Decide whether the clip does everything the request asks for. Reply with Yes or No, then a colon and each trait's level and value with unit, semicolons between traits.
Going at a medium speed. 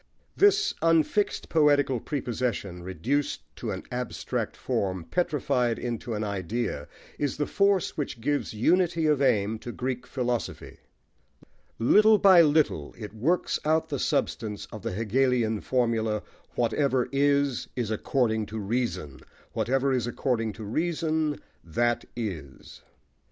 No: slow, 125 wpm